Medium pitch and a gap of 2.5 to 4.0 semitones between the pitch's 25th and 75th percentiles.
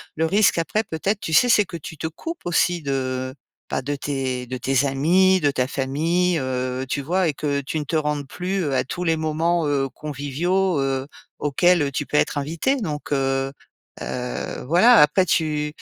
No: medium, 150 Hz; average, 4.4 semitones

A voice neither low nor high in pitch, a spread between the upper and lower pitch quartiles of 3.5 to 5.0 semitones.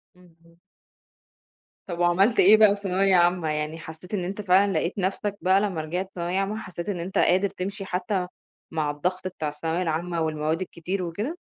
No: medium, 180 Hz; average, 2.7 semitones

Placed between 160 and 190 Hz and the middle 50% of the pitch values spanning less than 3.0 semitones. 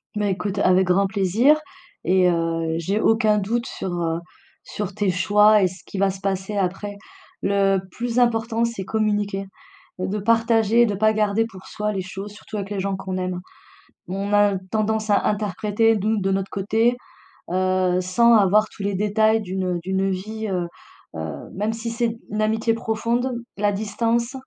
No: high, 205 Hz; narrow, 2.6 semitones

